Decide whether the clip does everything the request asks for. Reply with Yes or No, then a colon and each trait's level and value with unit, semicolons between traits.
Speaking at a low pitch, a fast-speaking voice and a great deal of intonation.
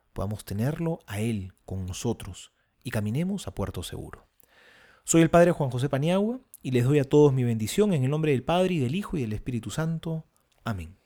Yes: low, 130 Hz; fast, 200 wpm; wide, 7.6 semitones